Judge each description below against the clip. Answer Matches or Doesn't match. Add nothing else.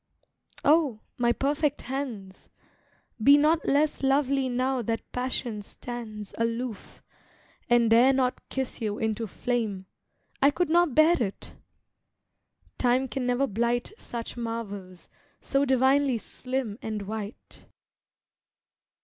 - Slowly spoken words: Matches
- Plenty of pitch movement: Doesn't match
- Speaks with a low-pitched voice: Doesn't match